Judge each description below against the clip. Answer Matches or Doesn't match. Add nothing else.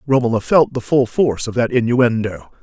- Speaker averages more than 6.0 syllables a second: Doesn't match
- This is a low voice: Matches